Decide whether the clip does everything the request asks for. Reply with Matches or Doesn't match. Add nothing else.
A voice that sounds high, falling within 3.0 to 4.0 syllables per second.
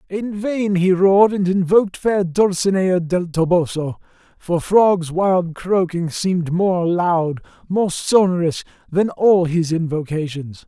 Doesn't match